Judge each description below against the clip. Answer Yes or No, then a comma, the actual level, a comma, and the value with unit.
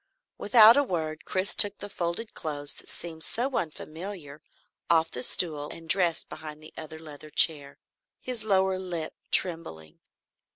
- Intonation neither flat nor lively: Yes, average, 3.8 semitones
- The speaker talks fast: No, average, 150 wpm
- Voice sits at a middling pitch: Yes, medium, 165 Hz